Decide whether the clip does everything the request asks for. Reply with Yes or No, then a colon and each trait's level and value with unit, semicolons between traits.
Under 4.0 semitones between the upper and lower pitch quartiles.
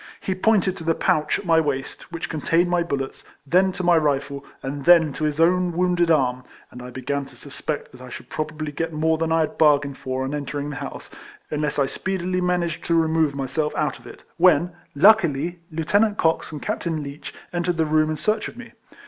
Yes: average, 3.4 semitones